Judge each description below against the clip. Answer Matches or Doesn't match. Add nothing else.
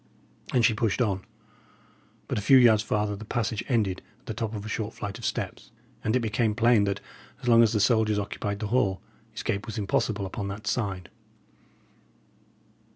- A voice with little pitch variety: Matches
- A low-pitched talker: Matches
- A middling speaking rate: Matches